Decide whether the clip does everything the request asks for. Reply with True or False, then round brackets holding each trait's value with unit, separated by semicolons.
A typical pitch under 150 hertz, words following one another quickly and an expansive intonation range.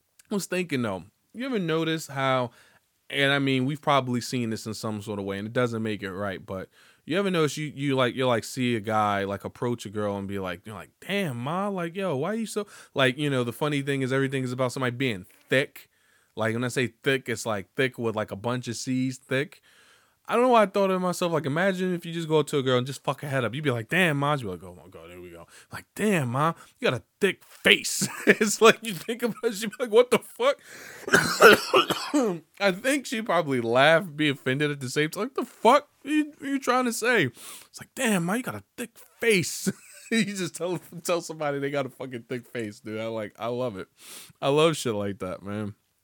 True (140 Hz; 255 wpm; 7.9 semitones)